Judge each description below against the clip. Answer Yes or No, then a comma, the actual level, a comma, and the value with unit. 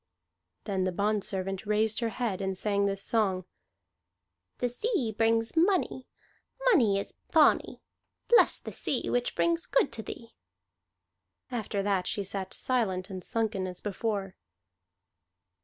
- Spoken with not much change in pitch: No, average, 3.6 semitones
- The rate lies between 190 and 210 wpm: No, slow, 135 wpm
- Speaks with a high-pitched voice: Yes, high, 210 Hz